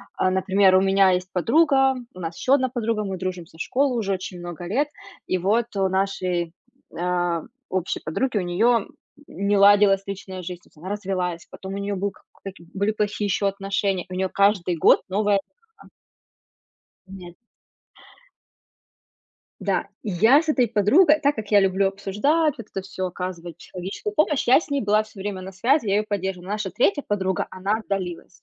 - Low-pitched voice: No, high, 195 Hz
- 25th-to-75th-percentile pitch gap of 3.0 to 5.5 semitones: No, narrow, 2.6 semitones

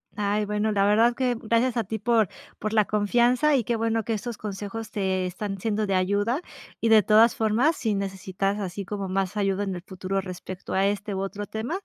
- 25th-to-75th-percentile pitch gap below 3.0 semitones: Yes, narrow, 2.5 semitones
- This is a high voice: Yes, high, 210 Hz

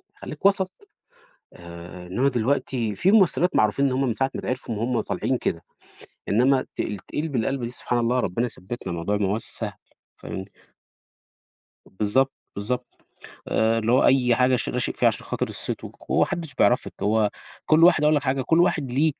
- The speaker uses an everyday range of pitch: Yes, average, 4.3 semitones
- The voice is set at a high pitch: No, low, 125 Hz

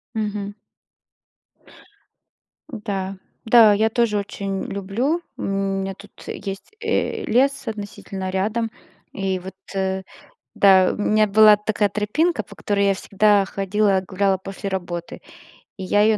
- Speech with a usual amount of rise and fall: No, narrow, 1.8 semitones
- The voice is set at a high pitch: Yes, high, 200 Hz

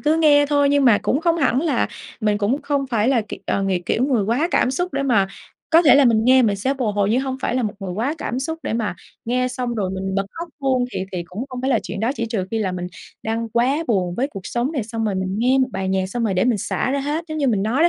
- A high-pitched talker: Yes, high, 240 Hz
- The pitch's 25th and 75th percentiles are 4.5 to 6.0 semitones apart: Yes, average, 4.9 semitones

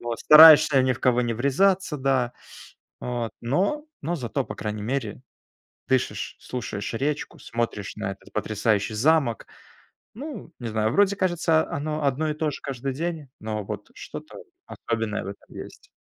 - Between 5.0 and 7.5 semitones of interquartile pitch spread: Yes, wide, 5.6 semitones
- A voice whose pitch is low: Yes, low, 130 Hz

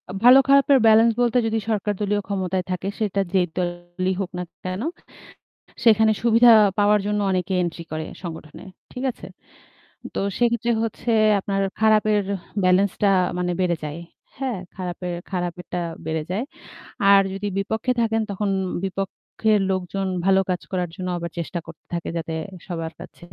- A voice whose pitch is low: No, high, 195 Hz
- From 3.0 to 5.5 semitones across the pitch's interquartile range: Yes, average, 3.5 semitones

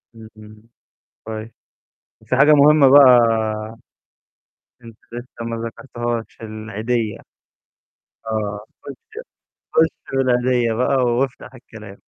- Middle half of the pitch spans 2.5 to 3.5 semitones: Yes, average, 3.1 semitones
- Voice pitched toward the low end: Yes, low, 120 Hz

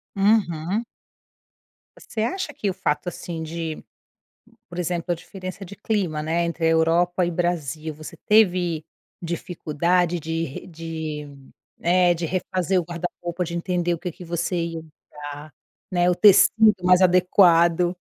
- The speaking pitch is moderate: Yes, medium, 175 Hz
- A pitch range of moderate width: No, narrow, 1.9 semitones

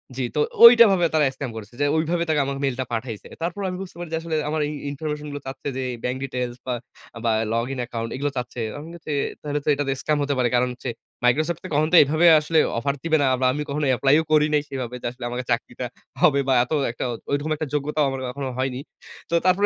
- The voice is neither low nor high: Yes, medium, 145 Hz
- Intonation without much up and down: No, average, 3.6 semitones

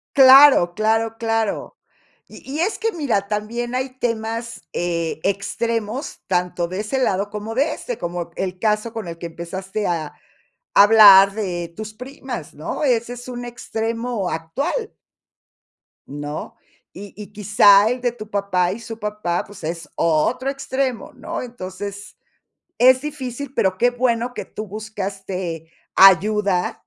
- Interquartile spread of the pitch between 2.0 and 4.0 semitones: No, average, 4.4 semitones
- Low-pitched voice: No, high, 215 Hz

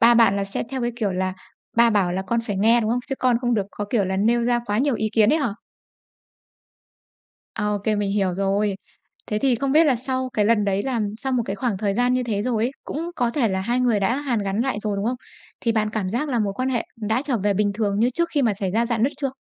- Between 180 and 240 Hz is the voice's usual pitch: Yes, high, 225 Hz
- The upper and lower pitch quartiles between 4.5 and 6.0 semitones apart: No, average, 3.4 semitones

